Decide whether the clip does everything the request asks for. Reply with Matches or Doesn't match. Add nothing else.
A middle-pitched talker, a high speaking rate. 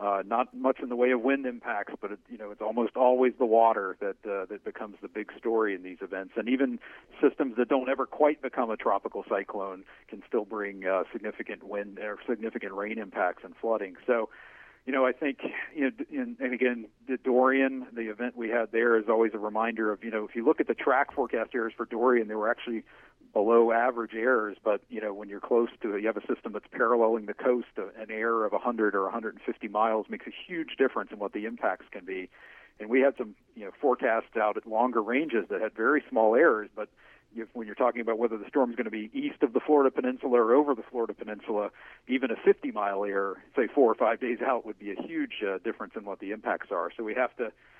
Doesn't match